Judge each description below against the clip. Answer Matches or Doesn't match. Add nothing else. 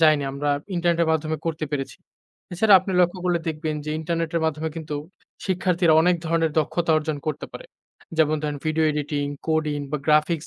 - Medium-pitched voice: Matches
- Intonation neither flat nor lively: Doesn't match